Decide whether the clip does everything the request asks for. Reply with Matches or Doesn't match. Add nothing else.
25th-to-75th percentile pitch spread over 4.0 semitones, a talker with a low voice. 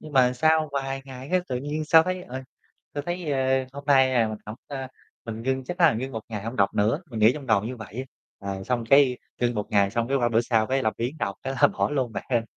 Doesn't match